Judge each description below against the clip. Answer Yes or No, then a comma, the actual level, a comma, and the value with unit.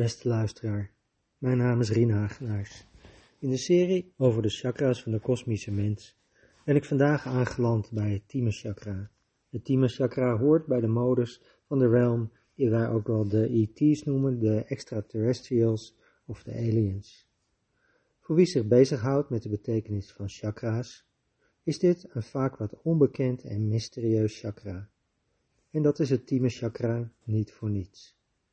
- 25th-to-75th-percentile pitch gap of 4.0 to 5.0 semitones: No, average, 3.3 semitones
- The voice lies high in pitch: No, low, 115 Hz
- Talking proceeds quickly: No, average, 155 wpm